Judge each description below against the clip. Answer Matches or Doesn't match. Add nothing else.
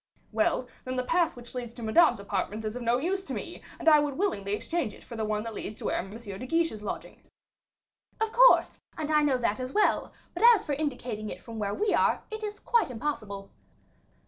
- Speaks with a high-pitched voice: Matches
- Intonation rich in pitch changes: Matches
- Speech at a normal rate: Doesn't match